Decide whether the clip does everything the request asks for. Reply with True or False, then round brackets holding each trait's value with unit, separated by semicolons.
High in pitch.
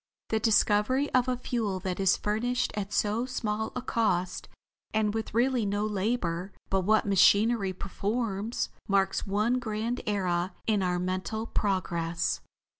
True (210 Hz)